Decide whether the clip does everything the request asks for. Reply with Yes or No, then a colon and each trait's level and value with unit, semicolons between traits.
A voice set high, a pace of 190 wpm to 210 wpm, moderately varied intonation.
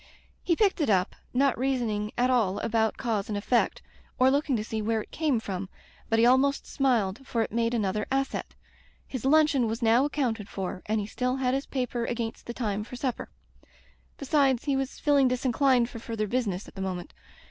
Yes: high, 240 Hz; average, 195 wpm; average, 3.7 semitones